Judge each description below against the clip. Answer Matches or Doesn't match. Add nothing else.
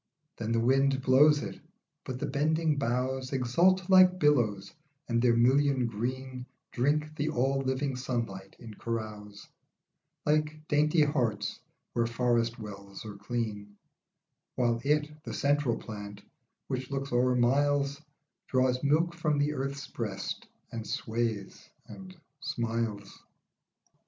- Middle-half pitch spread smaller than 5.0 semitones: Matches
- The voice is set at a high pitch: Doesn't match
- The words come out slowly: Matches